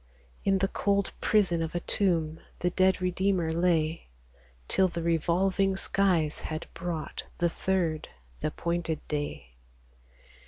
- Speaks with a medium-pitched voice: Yes, medium, 175 Hz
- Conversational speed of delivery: No, slow, 125 wpm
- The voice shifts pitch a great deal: No, average, 2.8 semitones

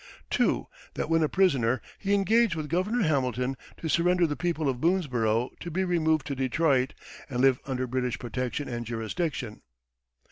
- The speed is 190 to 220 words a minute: No, average, 165 wpm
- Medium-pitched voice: Yes, medium, 145 Hz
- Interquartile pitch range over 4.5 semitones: Yes, wide, 5.4 semitones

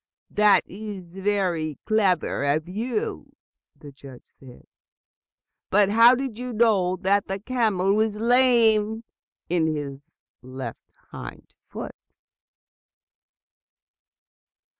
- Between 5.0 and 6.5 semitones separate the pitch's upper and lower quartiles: Yes, wide, 5.5 semitones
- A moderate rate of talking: No, slow, 95 wpm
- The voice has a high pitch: Yes, high, 200 Hz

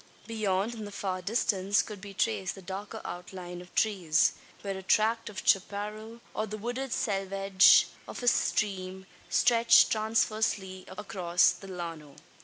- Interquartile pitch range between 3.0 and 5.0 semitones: No, narrow, 2.6 semitones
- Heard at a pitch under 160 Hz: No, high, 195 Hz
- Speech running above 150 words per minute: No, average, 145 wpm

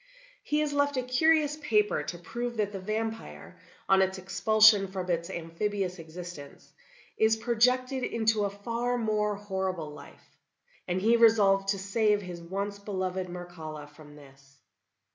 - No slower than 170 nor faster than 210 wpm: No, average, 145 wpm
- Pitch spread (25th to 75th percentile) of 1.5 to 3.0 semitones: No, average, 4.0 semitones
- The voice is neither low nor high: No, high, 200 Hz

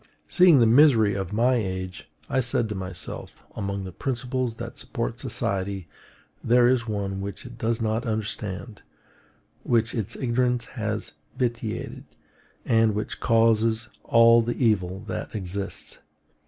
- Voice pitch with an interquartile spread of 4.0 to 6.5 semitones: No, average, 3.1 semitones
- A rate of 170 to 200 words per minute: No, slow, 135 wpm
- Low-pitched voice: Yes, low, 110 Hz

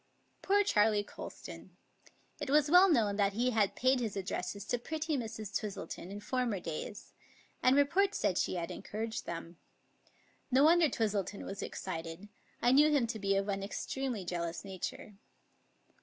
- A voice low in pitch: No, high, 215 Hz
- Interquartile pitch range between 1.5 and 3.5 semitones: No, average, 5.3 semitones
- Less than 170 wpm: Yes, average, 155 wpm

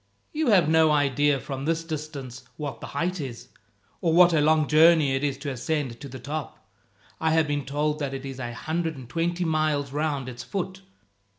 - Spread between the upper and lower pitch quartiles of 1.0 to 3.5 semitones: Yes, average, 2.8 semitones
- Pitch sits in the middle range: Yes, medium, 150 Hz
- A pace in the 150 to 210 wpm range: Yes, average, 200 wpm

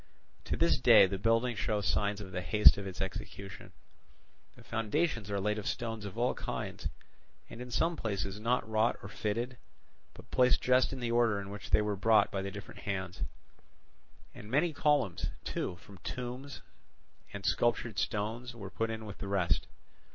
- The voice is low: Yes, low, 105 Hz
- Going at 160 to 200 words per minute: Yes, average, 180 wpm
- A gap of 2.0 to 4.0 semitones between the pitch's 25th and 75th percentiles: Yes, average, 3.3 semitones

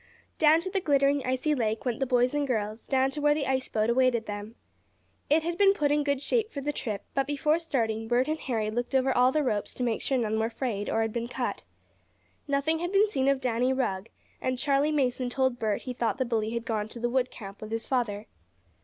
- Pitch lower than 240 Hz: No, very high, 255 Hz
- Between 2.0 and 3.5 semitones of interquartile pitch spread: No, average, 4.0 semitones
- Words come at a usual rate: No, fast, 240 wpm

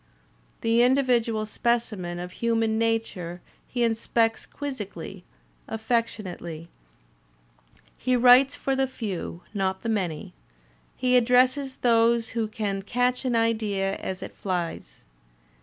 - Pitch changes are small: No, average, 4.1 semitones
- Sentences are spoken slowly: Yes, slow, 110 wpm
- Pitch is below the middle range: No, high, 225 Hz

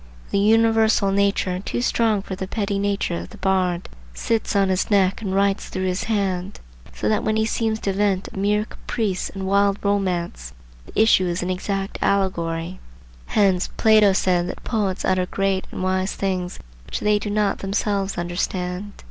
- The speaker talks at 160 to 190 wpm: Yes, average, 175 wpm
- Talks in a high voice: Yes, high, 195 Hz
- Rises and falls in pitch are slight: Yes, narrow, 1.8 semitones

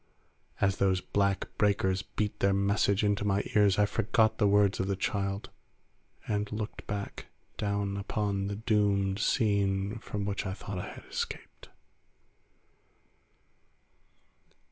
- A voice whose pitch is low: Yes, low, 100 Hz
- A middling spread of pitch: No, narrow, 0.9 semitones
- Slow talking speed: Yes, slow, 130 wpm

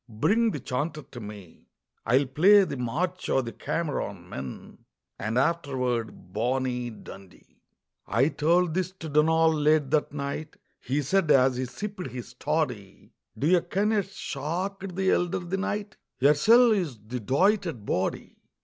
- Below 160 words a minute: Yes, average, 150 wpm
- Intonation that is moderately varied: No, wide, 6.5 semitones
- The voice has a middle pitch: Yes, medium, 150 Hz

